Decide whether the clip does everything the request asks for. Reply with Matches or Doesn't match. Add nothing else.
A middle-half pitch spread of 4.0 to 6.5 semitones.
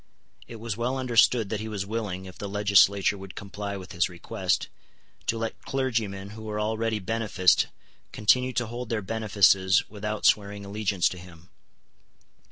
Doesn't match